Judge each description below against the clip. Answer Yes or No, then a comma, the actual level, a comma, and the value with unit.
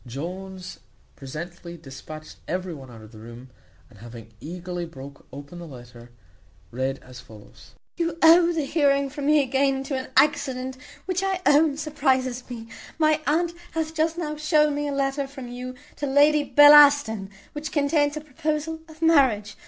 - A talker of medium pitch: No, very high, 270 Hz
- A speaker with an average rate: Yes, average, 165 wpm